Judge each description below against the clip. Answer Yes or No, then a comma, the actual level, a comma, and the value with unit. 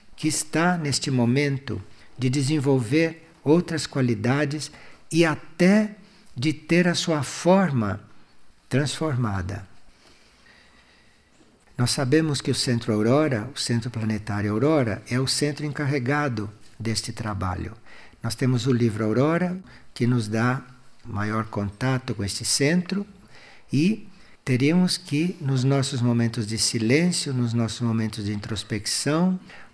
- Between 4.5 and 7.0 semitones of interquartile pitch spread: Yes, wide, 5.4 semitones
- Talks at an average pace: No, slow, 115 wpm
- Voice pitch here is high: No, low, 130 Hz